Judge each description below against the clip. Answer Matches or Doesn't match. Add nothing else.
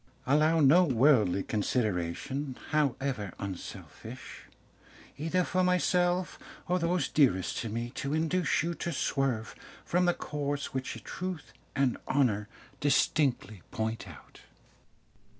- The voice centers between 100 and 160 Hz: Matches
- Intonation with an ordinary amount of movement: Doesn't match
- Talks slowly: Matches